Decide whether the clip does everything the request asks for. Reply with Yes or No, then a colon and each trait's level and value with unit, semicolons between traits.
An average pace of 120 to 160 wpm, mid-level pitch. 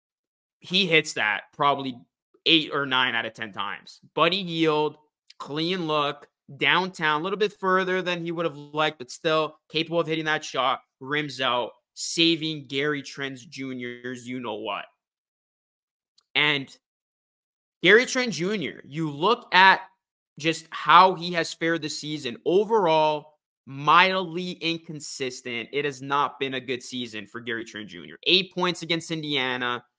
Yes: average, 140 wpm; medium, 155 Hz